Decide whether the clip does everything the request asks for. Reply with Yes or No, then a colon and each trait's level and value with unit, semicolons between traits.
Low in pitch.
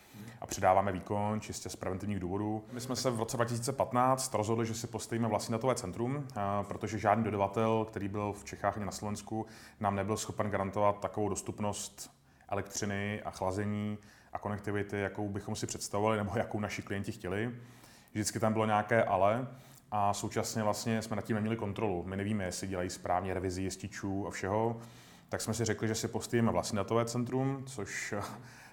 Yes: low, 105 Hz